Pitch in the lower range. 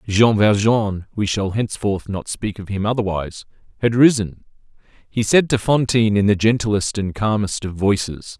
Yes: low, 105 Hz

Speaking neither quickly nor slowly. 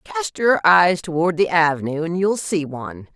Yes: average, 190 wpm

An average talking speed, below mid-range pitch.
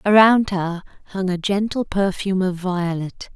No: average, 145 wpm; high, 190 Hz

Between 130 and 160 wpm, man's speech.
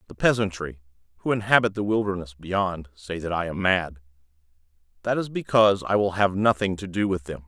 No: average, 185 wpm; male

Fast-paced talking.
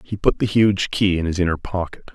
Yes: fast, 250 wpm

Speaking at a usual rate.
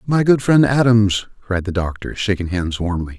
Yes: average, 190 wpm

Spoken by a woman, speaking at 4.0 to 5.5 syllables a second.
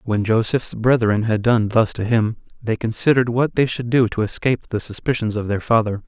No: male; 5.4 syllables/s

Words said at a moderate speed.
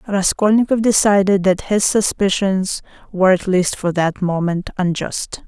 No: slow, 130 wpm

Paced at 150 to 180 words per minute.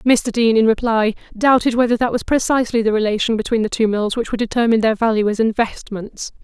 No: fast, 205 wpm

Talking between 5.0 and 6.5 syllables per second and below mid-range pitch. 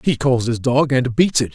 No: 4.8 syllables/s; low, 130 Hz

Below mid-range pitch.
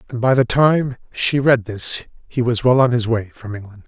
Yes: low, 120 Hz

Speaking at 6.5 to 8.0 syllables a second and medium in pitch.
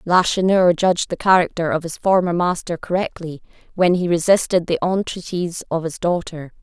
No: 5.2 syllables/s; medium, 175 Hz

